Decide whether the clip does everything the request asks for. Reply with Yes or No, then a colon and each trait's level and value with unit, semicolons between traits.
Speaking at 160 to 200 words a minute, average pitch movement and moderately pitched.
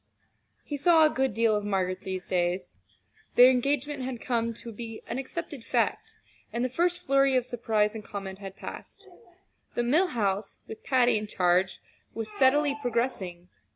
No: average, 165 wpm; average, 4.9 semitones; high, 235 Hz